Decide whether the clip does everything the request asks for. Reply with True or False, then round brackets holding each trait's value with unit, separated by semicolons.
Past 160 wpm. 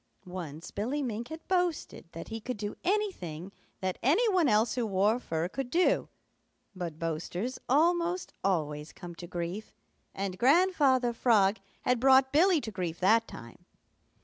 False (150 wpm)